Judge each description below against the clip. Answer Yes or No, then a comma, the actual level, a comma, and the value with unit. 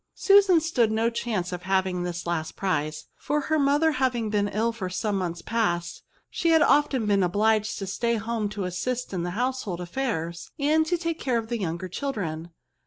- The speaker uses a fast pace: Yes, fast, 210 wpm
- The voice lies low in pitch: No, high, 215 Hz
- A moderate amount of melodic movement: No, wide, 6.4 semitones